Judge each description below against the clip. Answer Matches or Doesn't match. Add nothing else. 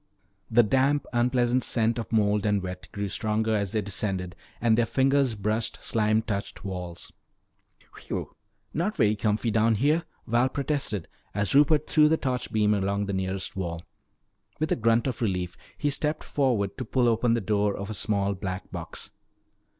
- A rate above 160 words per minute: Matches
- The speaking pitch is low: Matches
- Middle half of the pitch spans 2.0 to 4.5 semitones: Matches